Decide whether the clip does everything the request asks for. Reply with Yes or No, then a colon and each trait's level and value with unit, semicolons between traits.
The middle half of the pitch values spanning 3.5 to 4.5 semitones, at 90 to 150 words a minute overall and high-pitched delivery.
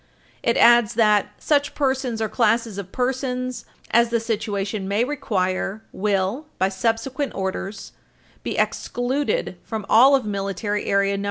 Yes: average, 4.1 semitones; average, 140 wpm; high, 225 Hz